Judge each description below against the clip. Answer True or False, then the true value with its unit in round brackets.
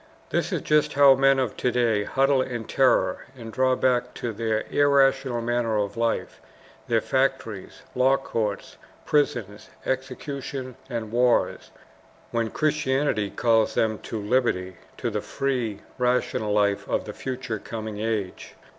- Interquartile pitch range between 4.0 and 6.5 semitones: False (3.3 semitones)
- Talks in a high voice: False (120 Hz)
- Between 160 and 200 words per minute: False (140 wpm)